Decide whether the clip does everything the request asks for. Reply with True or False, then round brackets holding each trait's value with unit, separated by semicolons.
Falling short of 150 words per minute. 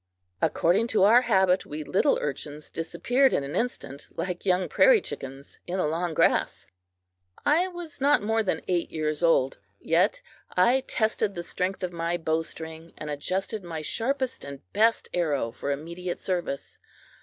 False (155 wpm)